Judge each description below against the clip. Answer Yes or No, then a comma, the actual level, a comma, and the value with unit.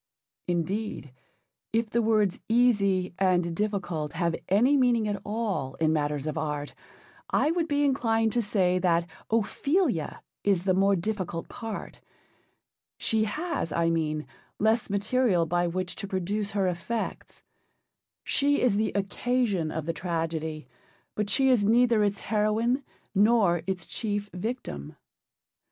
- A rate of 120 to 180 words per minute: Yes, slow, 135 wpm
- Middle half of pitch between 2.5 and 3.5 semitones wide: No, average, 4.7 semitones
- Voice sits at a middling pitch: No, high, 200 Hz